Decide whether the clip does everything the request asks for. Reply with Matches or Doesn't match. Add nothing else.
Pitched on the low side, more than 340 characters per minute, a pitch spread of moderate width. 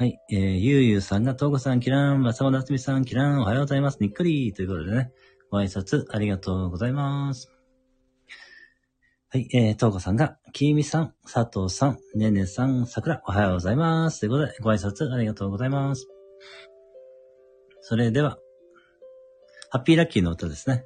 Matches